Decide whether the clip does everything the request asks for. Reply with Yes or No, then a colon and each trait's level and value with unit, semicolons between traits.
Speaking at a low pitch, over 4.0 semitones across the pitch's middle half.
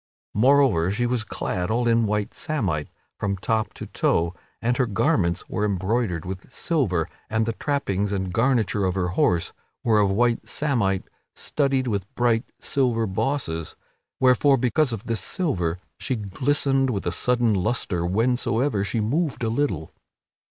Yes: low, 110 Hz; average, 5.0 semitones